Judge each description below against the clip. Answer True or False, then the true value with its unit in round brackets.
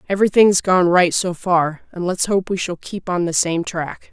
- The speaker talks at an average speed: False (220 wpm)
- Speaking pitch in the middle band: True (180 Hz)